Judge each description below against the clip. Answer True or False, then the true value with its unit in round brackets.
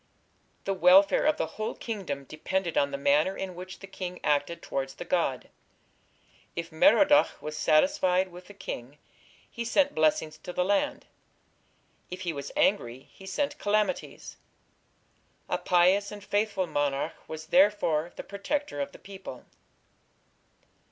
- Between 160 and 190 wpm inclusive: False (145 wpm)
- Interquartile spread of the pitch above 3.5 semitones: True (4.7 semitones)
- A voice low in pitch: False (180 Hz)